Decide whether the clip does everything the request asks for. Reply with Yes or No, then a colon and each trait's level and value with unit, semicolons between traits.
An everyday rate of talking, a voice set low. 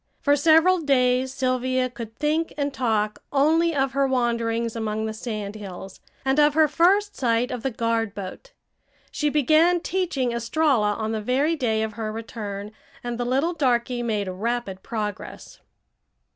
No: average, 160 wpm; very high, 250 Hz